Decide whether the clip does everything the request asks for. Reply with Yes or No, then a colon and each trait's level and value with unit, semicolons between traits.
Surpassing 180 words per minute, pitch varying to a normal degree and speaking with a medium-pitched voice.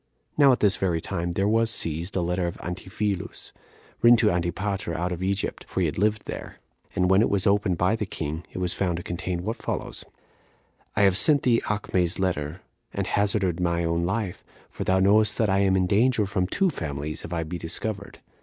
No: fast, 205 wpm; average, 3.1 semitones; very low, 95 Hz